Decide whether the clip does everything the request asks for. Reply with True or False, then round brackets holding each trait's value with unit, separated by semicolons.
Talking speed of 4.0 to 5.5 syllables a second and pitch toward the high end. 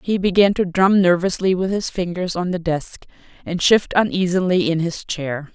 False (4.8 syllables/s; 180 Hz)